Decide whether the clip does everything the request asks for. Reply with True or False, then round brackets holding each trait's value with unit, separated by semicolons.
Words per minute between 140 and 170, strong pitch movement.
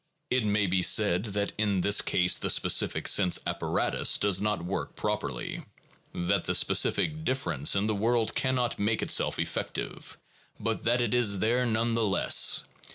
False (160 wpm; 3.2 semitones)